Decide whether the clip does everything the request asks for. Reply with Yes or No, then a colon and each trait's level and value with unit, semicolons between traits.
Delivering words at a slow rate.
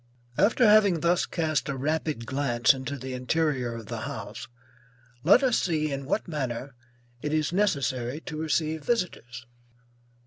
No: average, 145 wpm